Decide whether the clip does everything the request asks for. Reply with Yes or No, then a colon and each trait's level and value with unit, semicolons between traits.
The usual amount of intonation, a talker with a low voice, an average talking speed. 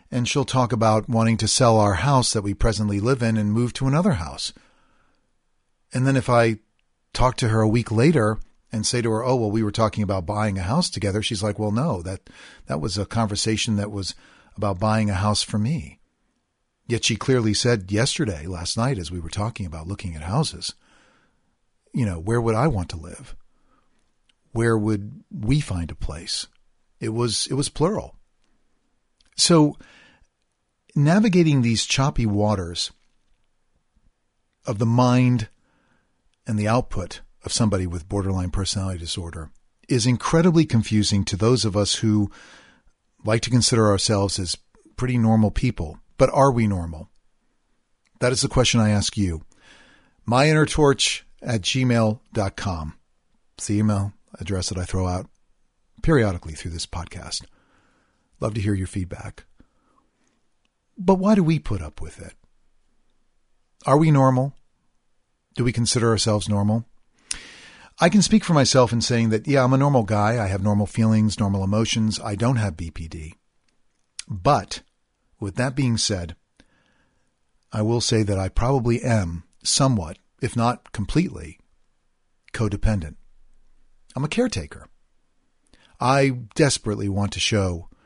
Yes: average, 3.9 semitones; low, 110 Hz; average, 150 wpm